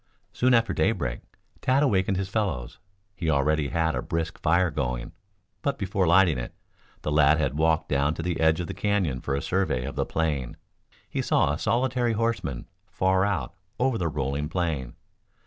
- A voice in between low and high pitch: No, very low, 80 Hz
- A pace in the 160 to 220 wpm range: Yes, average, 180 wpm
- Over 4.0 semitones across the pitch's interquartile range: Yes, wide, 5.4 semitones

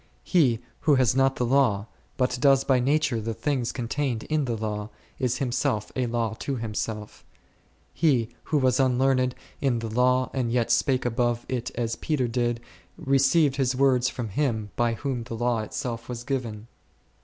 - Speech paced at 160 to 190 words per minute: Yes, average, 170 wpm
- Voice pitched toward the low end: Yes, low, 125 Hz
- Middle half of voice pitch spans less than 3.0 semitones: Yes, narrow, 2.6 semitones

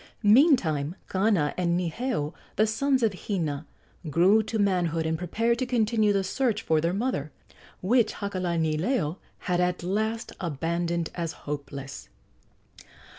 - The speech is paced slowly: Yes, slow, 125 wpm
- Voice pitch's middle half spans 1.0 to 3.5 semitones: No, average, 5.2 semitones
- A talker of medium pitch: Yes, medium, 180 Hz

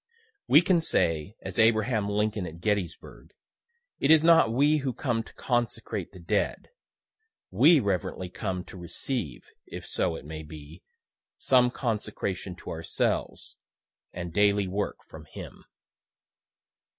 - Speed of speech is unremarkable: No, slow, 130 wpm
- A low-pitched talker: Yes, low, 105 Hz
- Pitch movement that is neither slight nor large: No, wide, 5.8 semitones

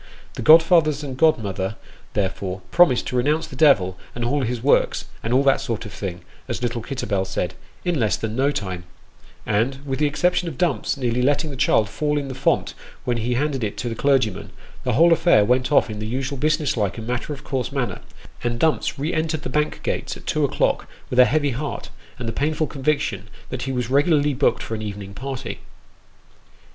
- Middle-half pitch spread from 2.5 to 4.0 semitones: No, average, 4.7 semitones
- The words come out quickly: Yes, fast, 215 wpm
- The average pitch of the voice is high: No, low, 130 Hz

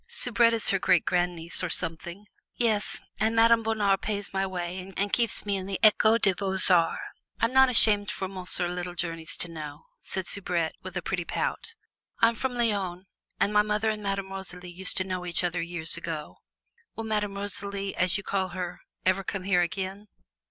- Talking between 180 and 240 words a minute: Yes, average, 185 wpm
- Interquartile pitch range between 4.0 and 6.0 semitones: No, average, 2.8 semitones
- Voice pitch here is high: Yes, high, 195 Hz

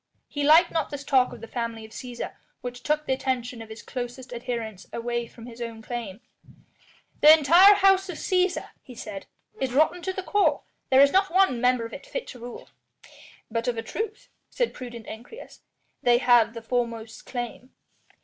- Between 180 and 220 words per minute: Yes, average, 190 wpm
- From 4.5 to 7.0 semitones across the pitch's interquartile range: Yes, average, 4.9 semitones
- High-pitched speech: Yes, very high, 250 Hz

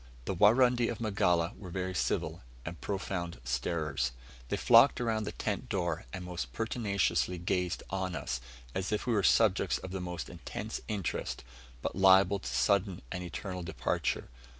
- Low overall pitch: Yes, very low, 95 Hz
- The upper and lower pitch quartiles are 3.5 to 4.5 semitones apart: No, average, 3.1 semitones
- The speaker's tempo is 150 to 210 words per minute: Yes, average, 155 wpm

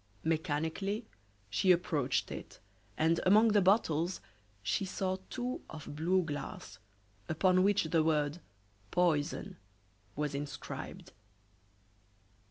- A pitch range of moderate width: Yes, average, 4.0 semitones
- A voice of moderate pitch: Yes, medium, 165 Hz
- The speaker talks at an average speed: No, slow, 100 wpm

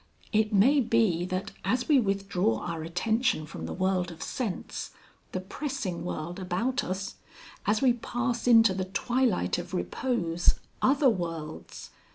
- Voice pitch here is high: Yes, high, 195 Hz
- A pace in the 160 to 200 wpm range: No, average, 145 wpm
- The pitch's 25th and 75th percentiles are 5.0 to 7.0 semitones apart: Yes, wide, 5.4 semitones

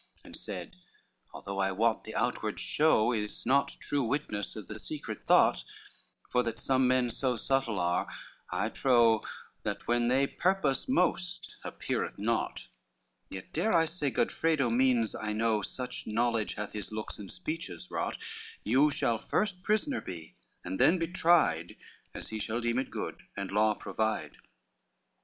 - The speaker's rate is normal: Yes, average, 160 wpm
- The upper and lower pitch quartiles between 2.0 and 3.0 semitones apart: No, average, 4.8 semitones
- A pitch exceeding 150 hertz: No, low, 120 Hz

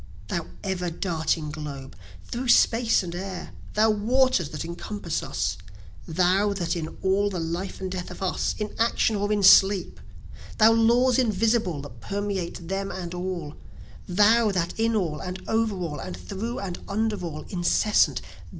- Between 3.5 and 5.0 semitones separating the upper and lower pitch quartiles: Yes, average, 3.8 semitones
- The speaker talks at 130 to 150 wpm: No, average, 160 wpm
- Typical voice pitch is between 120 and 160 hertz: No, high, 190 Hz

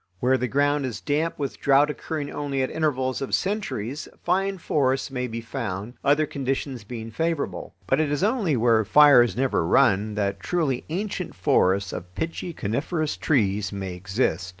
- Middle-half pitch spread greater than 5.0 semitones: Yes, wide, 5.6 semitones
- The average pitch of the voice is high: No, low, 130 Hz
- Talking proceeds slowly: No, average, 165 wpm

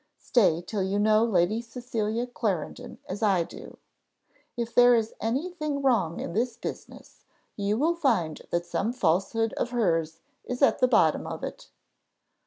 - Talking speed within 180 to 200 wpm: No, average, 160 wpm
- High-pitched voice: Yes, high, 225 Hz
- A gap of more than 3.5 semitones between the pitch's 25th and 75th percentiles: Yes, average, 4.6 semitones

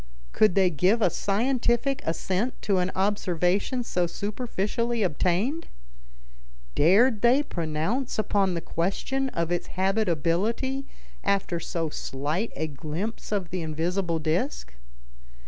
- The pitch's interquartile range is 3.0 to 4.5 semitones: No, average, 5.3 semitones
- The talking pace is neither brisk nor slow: No, slow, 115 wpm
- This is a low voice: No, high, 190 Hz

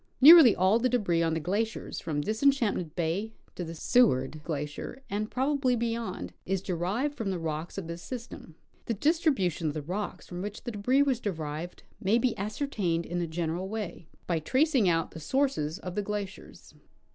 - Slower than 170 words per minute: No, average, 180 wpm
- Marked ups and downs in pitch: Yes, wide, 6.1 semitones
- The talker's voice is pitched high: Yes, high, 195 Hz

